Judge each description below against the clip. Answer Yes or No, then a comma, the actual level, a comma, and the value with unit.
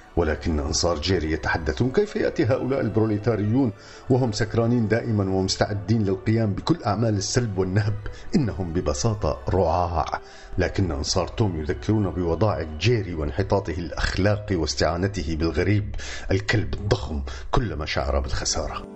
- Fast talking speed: No, average, 110 wpm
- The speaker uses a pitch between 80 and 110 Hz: Yes, low, 100 Hz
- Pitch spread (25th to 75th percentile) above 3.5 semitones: Yes, average, 4.2 semitones